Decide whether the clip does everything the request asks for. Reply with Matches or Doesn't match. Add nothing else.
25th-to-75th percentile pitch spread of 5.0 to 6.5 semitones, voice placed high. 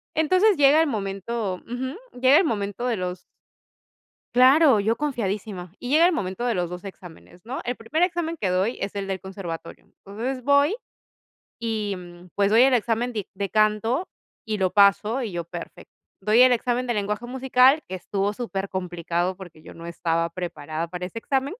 Matches